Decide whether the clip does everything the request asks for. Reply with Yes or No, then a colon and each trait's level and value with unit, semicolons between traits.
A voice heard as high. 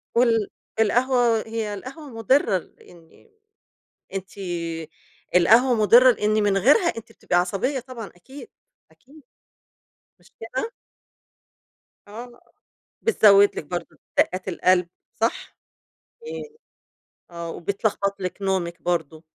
Yes: high, 210 Hz